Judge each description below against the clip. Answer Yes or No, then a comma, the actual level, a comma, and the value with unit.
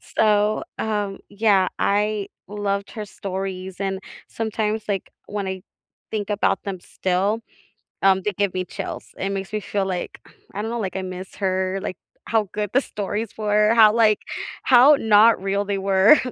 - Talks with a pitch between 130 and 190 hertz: No, high, 205 Hz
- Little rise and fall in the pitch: Yes, narrow, 1.8 semitones